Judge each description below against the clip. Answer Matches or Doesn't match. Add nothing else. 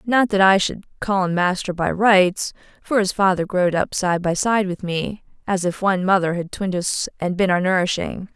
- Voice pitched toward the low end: Doesn't match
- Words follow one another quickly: Matches